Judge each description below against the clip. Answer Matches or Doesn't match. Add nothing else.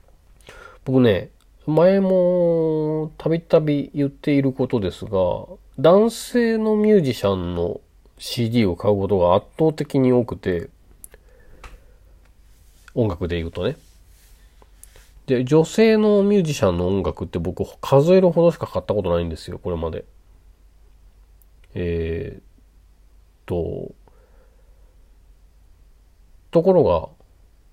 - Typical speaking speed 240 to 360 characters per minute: Doesn't match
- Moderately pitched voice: Doesn't match